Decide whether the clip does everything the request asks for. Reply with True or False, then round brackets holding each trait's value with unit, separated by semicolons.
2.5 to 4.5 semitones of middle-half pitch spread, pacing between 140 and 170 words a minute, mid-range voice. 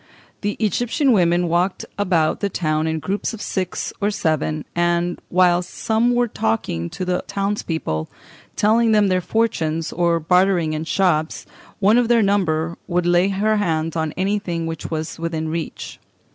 True (4.0 semitones; 160 wpm; 175 Hz)